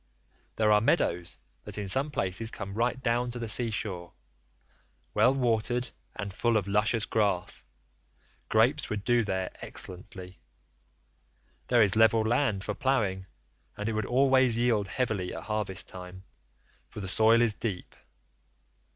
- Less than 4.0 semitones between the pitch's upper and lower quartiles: Yes, average, 3.5 semitones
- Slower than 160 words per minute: Yes, average, 145 wpm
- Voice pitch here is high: No, low, 110 Hz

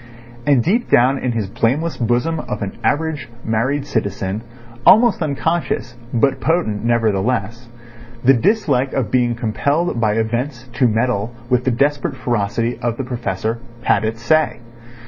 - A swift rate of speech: No, average, 145 wpm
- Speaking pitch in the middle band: No, low, 125 Hz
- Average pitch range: Yes, average, 4.0 semitones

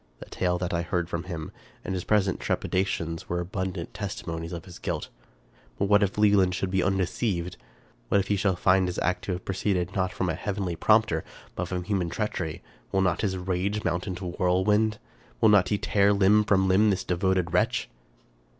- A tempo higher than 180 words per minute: Yes, average, 200 wpm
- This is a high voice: No, very low, 95 Hz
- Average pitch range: No, narrow, 2.2 semitones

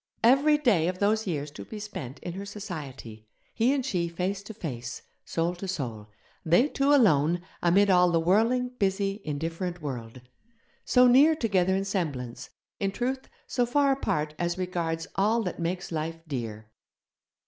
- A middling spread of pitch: No, wide, 5.7 semitones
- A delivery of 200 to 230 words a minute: No, average, 160 wpm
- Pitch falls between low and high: Yes, medium, 180 Hz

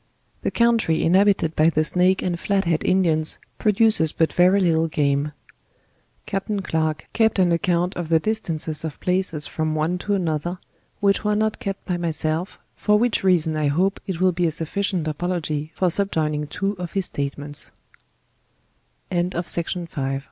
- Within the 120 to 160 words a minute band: Yes, average, 140 wpm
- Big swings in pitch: No, average, 3.7 semitones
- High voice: No, medium, 175 Hz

